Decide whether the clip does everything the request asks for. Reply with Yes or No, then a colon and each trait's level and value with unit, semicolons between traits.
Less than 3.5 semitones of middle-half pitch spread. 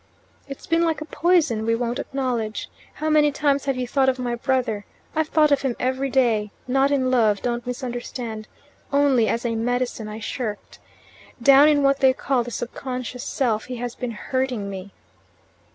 Yes: average, 3.0 semitones